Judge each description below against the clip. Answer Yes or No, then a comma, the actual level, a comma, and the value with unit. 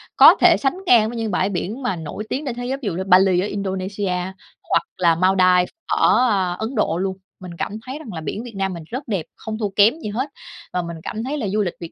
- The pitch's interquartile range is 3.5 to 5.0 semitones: Yes, average, 4.3 semitones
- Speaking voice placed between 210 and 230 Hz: No, high, 200 Hz